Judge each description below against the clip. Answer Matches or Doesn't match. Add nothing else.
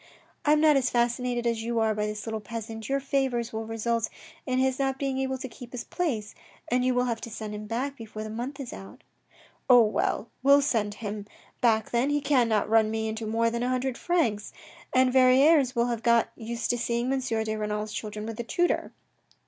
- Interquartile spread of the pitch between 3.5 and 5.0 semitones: Doesn't match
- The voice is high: Matches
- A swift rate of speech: Matches